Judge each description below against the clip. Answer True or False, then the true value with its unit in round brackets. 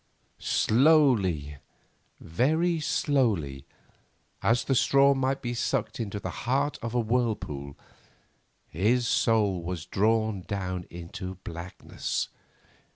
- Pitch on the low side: True (110 Hz)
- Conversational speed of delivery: False (100 wpm)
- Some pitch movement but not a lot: False (6.1 semitones)